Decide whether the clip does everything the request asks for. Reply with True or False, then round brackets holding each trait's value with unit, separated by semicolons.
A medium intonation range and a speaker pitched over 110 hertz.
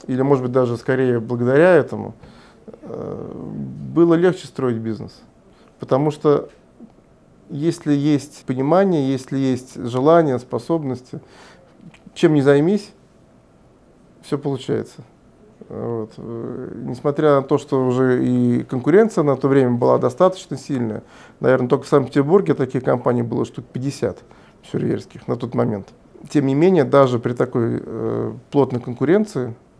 True (3.0 semitones; 135 Hz)